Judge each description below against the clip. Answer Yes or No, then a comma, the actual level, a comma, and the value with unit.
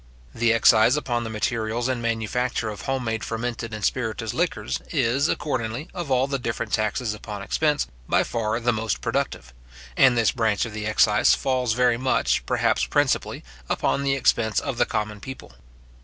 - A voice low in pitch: Yes, low, 115 Hz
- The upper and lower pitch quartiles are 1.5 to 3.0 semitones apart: Yes, narrow, 2.6 semitones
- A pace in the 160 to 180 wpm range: Yes, average, 170 wpm